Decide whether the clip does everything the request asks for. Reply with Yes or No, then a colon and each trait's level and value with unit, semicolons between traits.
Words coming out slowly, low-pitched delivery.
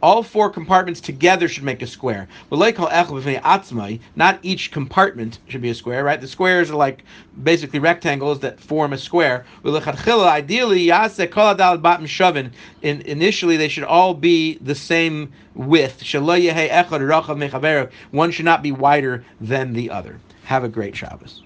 No: slow, 130 wpm; medium, 150 Hz